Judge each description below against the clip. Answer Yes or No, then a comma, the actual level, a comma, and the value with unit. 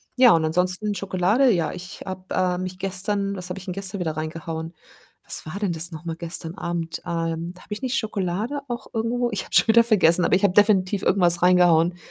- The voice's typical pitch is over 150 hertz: Yes, medium, 185 Hz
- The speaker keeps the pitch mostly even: No, average, 3.0 semitones